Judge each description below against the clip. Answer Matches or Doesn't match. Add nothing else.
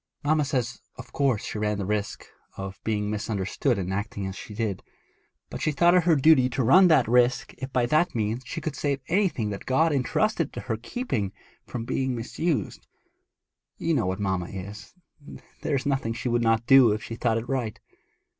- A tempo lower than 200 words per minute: Doesn't match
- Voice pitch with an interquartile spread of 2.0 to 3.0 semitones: Doesn't match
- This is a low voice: Matches